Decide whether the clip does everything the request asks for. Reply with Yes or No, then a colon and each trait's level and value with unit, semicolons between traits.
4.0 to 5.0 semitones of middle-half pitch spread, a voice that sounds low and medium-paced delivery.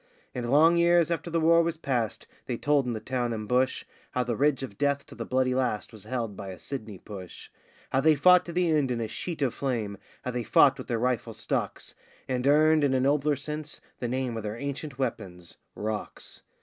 No: average, 4.4 semitones; low, 130 Hz; fast, 220 wpm